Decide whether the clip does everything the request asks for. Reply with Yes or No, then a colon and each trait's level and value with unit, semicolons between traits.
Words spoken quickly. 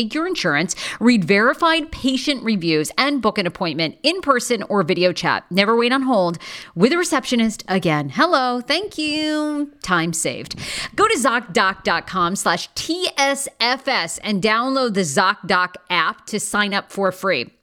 No: average, 140 wpm